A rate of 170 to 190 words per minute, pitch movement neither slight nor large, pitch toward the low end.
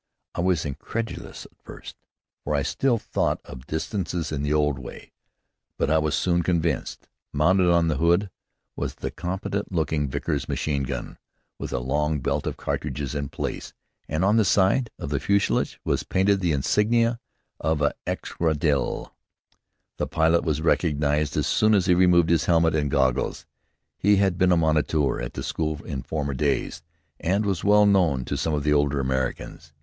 Yes: average, 175 wpm; average, 4.2 semitones; very low, 80 Hz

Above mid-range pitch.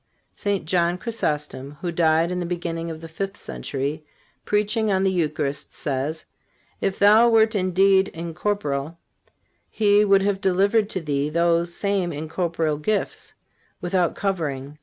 No: medium, 175 Hz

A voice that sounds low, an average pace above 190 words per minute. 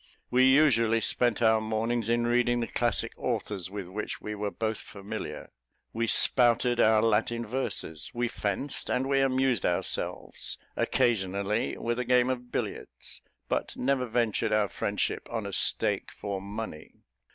No: low, 115 Hz; average, 150 wpm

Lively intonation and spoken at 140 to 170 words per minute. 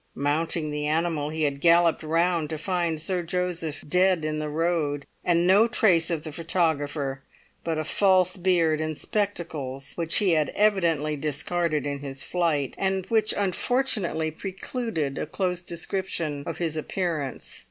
No: average, 3.0 semitones; average, 150 wpm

